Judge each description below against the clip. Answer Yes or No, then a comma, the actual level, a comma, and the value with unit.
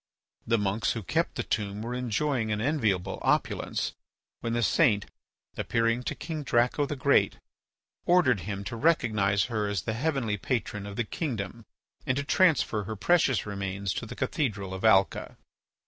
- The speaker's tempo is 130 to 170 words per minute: Yes, average, 165 wpm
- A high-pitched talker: No, low, 115 Hz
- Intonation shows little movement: No, average, 4.2 semitones